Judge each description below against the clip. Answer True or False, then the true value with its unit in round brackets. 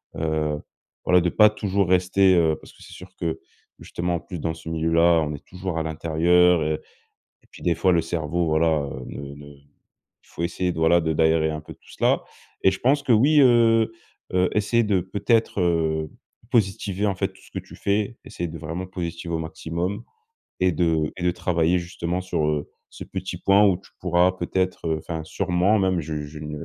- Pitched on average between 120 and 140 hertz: False (85 Hz)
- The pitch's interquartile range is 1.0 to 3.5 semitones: True (2.8 semitones)